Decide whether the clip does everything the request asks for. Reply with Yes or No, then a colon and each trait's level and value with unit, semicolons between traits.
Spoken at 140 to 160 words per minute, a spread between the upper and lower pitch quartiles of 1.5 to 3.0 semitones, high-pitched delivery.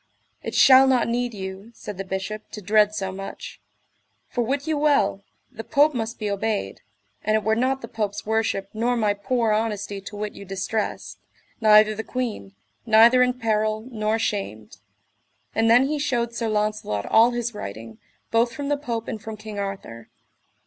No: average, 175 wpm; average, 2.7 semitones; high, 220 Hz